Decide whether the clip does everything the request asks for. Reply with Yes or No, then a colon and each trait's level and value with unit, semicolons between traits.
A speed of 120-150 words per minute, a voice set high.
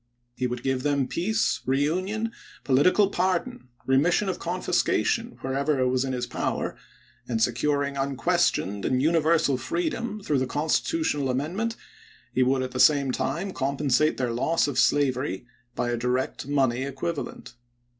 No: average, 145 wpm; medium, 140 Hz